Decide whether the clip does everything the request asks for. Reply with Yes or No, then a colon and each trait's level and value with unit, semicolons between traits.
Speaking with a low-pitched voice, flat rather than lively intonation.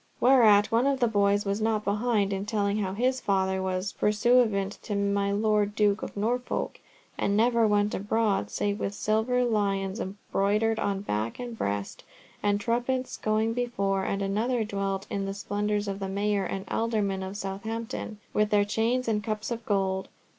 No: high, 205 Hz; narrow, 2.1 semitones